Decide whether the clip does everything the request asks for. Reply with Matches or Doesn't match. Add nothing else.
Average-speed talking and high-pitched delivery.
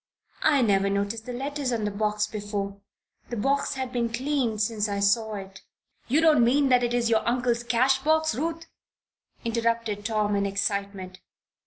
Matches